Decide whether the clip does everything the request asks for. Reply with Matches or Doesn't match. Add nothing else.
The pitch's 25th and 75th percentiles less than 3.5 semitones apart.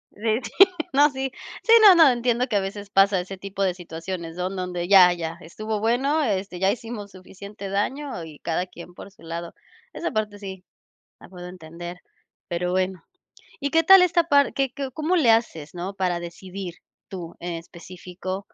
Doesn't match